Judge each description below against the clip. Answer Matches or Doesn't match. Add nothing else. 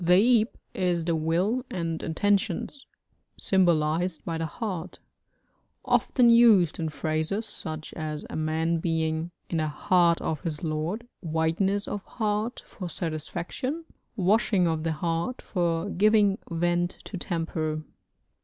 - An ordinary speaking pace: Doesn't match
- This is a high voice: Doesn't match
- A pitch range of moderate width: Matches